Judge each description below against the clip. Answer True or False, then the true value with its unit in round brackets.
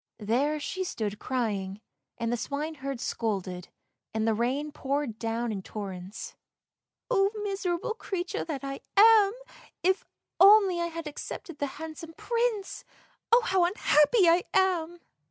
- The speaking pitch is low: False (300 Hz)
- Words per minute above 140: False (135 wpm)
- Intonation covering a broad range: True (8.3 semitones)